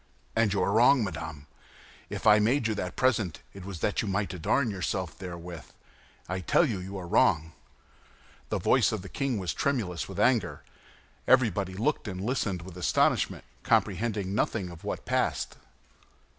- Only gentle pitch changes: No, average, 3.8 semitones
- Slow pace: No, average, 170 wpm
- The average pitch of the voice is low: Yes, very low, 95 Hz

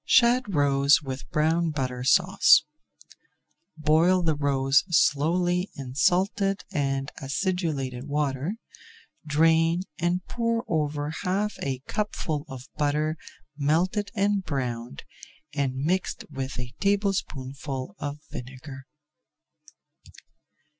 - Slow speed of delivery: Yes, slow, 100 wpm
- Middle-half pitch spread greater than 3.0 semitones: Yes, average, 4.9 semitones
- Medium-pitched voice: Yes, medium, 150 Hz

